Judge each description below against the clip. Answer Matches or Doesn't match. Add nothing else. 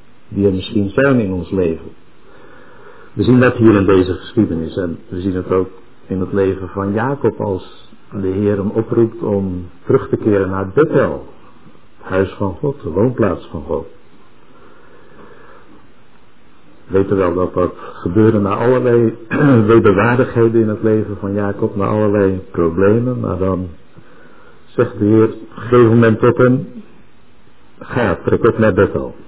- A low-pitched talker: Matches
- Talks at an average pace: Matches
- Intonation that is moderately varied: Matches